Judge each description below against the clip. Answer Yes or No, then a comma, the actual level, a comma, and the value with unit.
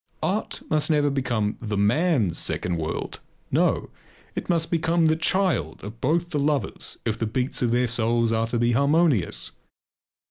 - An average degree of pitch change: No, wide, 5.9 semitones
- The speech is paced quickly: No, average, 165 wpm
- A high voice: No, low, 125 Hz